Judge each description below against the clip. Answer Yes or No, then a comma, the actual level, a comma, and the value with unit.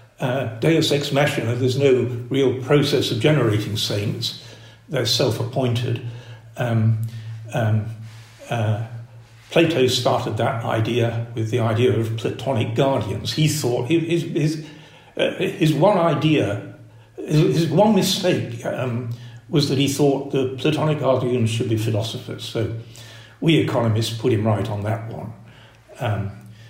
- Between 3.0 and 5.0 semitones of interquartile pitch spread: Yes, average, 4.0 semitones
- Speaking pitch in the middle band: No, low, 120 Hz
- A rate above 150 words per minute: No, average, 140 wpm